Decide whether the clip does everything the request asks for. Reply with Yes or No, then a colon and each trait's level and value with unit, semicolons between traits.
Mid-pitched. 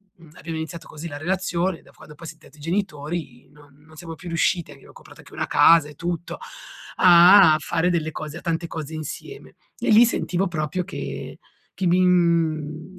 Yes: medium, 165 Hz